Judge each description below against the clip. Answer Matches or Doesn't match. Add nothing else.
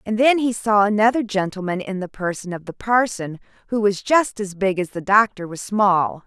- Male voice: Doesn't match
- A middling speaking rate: Doesn't match